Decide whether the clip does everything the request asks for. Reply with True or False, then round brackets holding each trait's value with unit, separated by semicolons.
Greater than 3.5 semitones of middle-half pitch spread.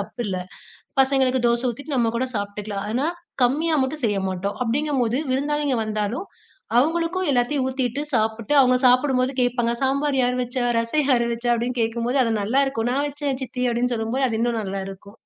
False (3.1 semitones)